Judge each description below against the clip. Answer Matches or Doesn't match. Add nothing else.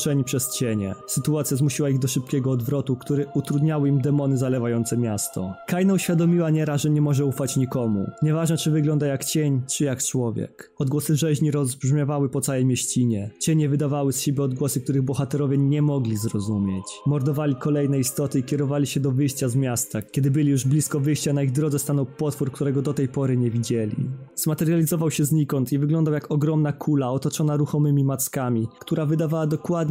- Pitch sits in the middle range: Matches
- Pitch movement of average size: Doesn't match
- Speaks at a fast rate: Matches